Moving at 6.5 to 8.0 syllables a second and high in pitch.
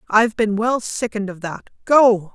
No: 5.0 syllables/s; high, 215 Hz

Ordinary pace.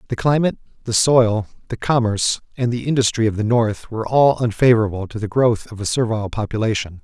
Yes: average, 190 wpm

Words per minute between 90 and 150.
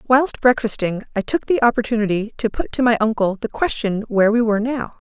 No: average, 200 wpm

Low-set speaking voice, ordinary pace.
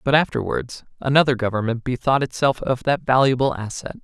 Yes: low, 130 Hz; average, 150 wpm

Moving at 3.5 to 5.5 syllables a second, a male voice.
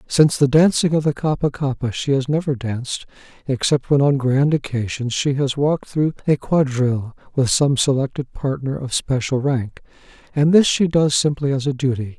Yes: 5.1 syllables/s; male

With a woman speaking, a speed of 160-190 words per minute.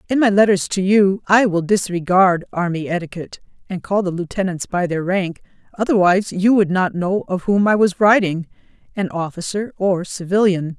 Yes: female; average, 165 wpm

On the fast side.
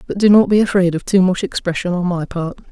Yes: fast, 265 wpm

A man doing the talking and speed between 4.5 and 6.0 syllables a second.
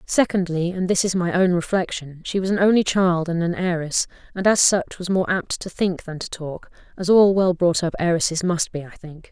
No: female; 5.1 syllables/s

